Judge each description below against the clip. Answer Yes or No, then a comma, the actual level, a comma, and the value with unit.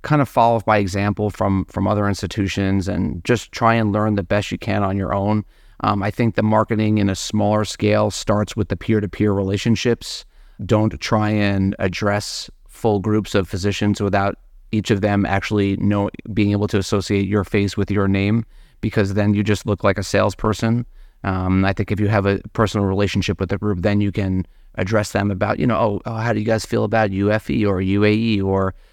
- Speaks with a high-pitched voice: No, low, 105 Hz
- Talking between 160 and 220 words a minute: Yes, fast, 205 wpm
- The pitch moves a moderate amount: No, narrow, 1.4 semitones